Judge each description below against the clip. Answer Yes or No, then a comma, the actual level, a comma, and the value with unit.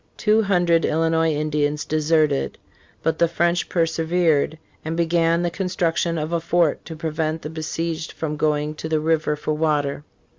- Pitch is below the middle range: No, medium, 160 Hz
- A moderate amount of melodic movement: No, narrow, 1.6 semitones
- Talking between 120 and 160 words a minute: Yes, average, 155 wpm